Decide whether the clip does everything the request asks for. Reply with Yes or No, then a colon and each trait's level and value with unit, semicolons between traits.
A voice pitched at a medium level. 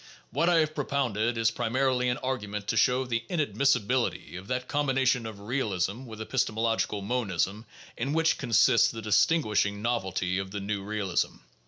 No: low, 115 Hz